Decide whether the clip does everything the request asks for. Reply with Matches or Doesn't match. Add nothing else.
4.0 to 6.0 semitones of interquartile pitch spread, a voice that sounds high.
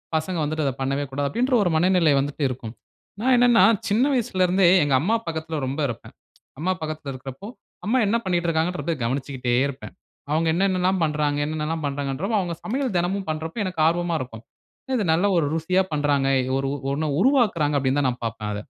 Doesn't match